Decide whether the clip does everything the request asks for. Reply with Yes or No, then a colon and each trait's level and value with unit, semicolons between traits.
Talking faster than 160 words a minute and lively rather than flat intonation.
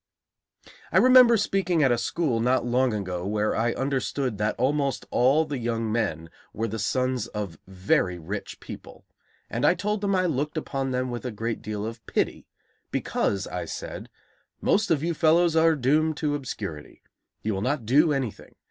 Yes: average, 175 wpm; wide, 6.2 semitones